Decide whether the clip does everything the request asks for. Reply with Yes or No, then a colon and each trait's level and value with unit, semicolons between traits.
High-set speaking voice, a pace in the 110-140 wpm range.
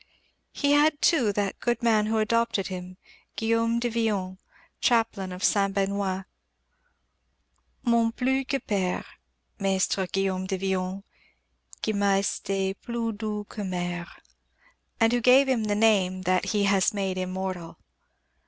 Yes: high, 200 Hz; slow, 135 wpm